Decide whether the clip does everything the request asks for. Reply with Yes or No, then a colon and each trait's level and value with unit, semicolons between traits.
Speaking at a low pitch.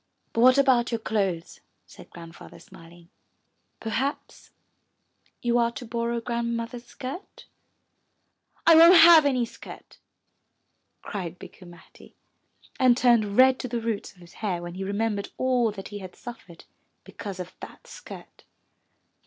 No: high, 230 Hz